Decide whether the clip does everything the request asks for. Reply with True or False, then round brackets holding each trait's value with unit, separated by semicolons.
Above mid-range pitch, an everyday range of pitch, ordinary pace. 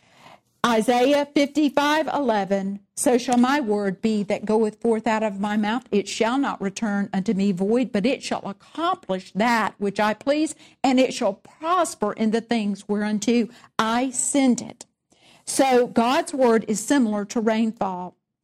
True (225 Hz; 3.8 semitones; 155 wpm)